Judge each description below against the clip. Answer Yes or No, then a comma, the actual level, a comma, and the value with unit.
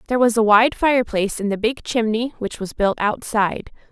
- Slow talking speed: No, average, 200 wpm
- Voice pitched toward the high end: Yes, high, 225 Hz